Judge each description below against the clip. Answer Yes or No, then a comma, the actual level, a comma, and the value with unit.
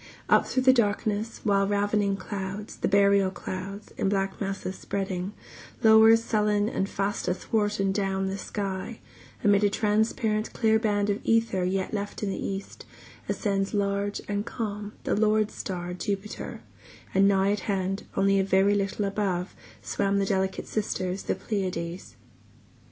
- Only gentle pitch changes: Yes, narrow, 1.5 semitones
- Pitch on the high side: Yes, high, 200 Hz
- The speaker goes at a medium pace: Yes, average, 150 wpm